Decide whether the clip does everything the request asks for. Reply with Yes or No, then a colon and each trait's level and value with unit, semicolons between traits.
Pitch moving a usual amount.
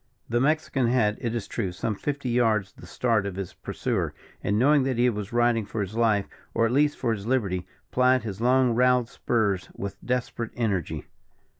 Yes: average, 3.5 semitones